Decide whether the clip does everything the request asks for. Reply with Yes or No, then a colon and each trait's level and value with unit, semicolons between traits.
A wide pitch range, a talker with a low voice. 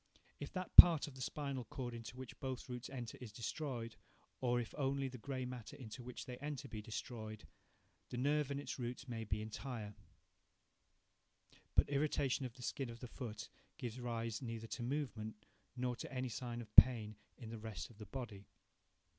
No: average, 2.8 semitones; low, 125 Hz